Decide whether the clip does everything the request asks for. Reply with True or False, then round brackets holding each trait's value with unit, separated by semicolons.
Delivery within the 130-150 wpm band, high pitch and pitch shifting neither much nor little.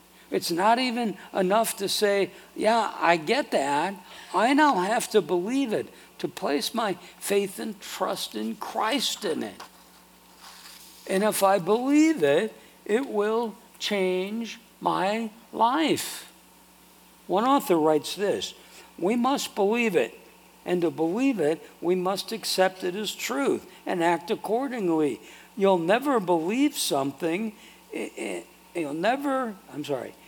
True (135 wpm; 205 Hz; 4.1 semitones)